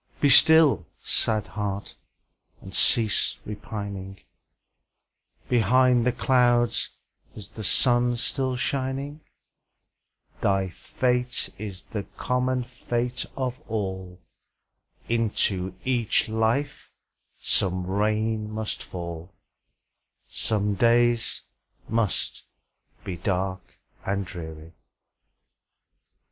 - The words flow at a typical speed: No, slow, 85 wpm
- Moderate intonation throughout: Yes, average, 4.2 semitones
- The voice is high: No, low, 110 Hz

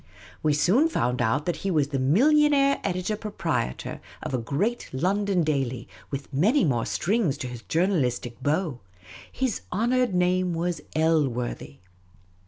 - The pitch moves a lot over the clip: Yes, wide, 7.2 semitones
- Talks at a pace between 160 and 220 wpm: No, average, 140 wpm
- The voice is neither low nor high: Yes, medium, 165 Hz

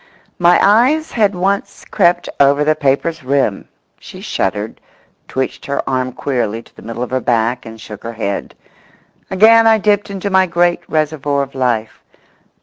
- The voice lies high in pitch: No, medium, 145 Hz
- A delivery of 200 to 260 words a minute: No, average, 165 wpm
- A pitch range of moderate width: No, wide, 7.5 semitones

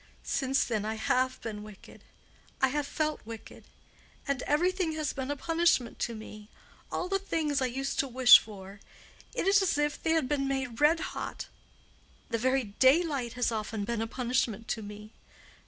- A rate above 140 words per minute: Yes, average, 170 wpm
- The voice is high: Yes, very high, 260 Hz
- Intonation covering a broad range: No, average, 4.7 semitones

